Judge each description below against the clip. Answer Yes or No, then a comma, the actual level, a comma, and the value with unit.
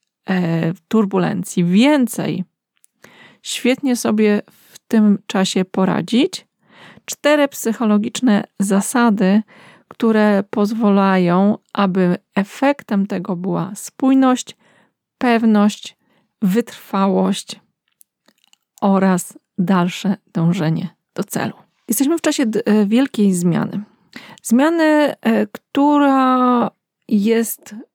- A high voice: Yes, high, 210 Hz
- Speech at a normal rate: No, slow, 70 wpm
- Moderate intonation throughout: Yes, average, 3.9 semitones